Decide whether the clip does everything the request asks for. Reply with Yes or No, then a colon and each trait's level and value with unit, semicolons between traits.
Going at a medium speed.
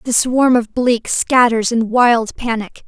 Yes: average, 165 wpm